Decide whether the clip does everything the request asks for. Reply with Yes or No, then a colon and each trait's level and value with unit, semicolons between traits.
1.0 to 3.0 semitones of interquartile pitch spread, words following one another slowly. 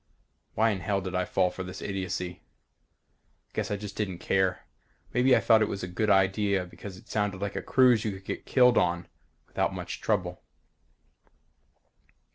No: narrow, 2.5 semitones; average, 175 wpm